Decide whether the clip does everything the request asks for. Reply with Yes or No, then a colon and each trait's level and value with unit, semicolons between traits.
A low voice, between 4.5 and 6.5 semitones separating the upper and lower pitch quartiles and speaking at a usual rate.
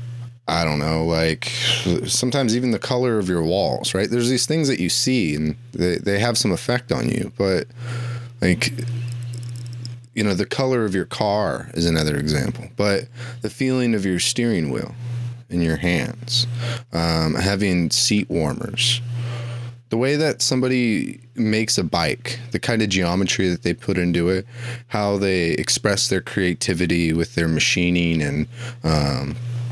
Yes: low, 115 Hz; average, 5.3 semitones; average, 160 wpm